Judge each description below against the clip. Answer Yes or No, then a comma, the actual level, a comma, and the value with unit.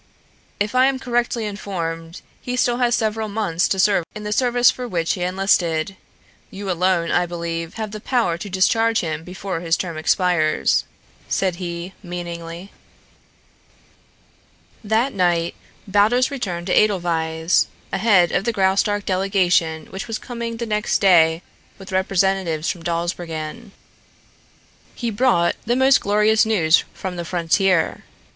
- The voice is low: No, high, 190 Hz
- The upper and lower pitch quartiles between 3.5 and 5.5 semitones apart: Yes, average, 4.1 semitones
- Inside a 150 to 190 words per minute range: No, average, 140 wpm